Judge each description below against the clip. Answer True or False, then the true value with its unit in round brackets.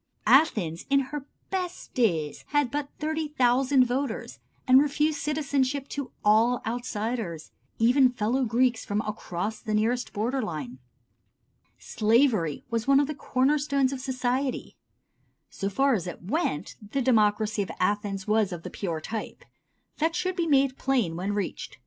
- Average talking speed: True (150 wpm)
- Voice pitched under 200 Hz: False (245 Hz)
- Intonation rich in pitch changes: False (5.0 semitones)